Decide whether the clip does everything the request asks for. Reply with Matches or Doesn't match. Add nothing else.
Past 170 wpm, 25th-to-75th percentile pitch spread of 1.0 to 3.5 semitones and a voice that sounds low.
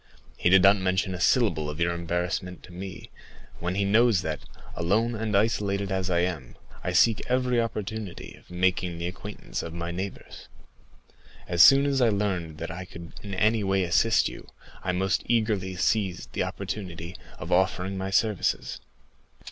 Doesn't match